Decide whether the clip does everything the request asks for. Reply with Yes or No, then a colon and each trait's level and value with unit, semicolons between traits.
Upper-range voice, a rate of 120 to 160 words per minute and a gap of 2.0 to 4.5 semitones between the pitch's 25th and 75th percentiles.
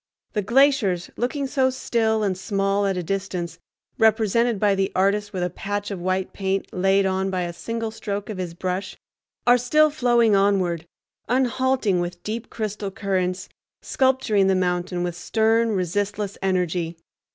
Yes: high, 200 Hz; average, 155 wpm; average, 3.4 semitones